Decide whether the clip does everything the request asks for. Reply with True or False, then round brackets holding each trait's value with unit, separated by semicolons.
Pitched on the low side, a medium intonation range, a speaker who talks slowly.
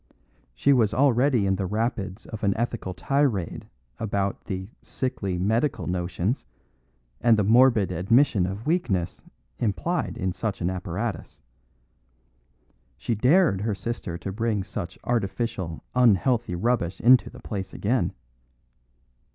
True (105 Hz; 4.3 semitones; 125 wpm)